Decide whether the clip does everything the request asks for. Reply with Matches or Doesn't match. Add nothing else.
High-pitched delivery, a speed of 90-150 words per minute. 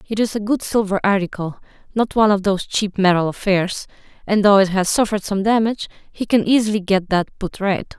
Doesn't match